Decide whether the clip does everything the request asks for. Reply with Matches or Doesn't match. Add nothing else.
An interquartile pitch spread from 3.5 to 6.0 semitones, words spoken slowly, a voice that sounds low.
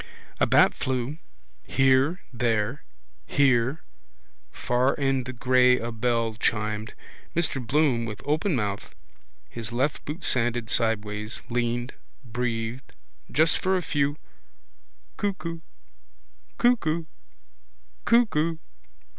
Matches